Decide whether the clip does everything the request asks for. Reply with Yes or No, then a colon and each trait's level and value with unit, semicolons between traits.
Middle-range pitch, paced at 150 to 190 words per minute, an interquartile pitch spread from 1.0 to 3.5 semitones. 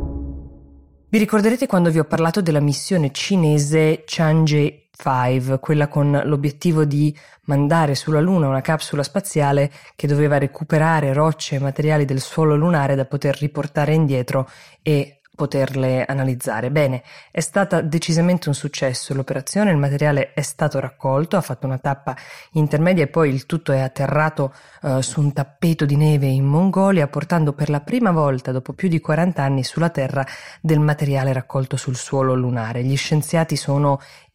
Yes: medium, 145 Hz; average, 155 wpm; average, 2.7 semitones